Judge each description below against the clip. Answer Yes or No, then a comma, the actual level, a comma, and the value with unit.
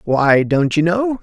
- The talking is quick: No, average, 195 wpm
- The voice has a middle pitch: Yes, medium, 170 Hz